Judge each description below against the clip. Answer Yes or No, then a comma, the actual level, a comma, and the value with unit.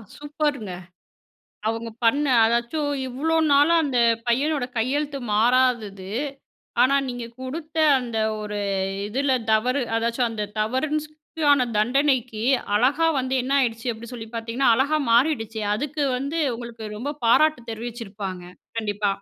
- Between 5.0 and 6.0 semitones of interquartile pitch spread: No, average, 4.1 semitones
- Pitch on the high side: Yes, high, 245 Hz